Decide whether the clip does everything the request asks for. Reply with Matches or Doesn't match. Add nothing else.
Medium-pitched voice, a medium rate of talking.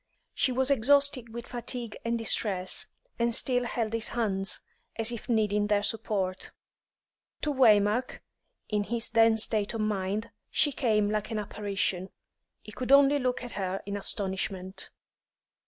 Doesn't match